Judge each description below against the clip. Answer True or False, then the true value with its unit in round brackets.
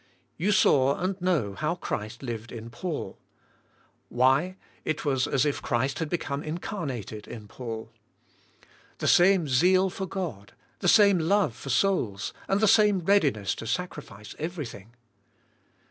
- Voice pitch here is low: False (150 Hz)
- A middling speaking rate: False (130 wpm)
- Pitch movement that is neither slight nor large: False (7.7 semitones)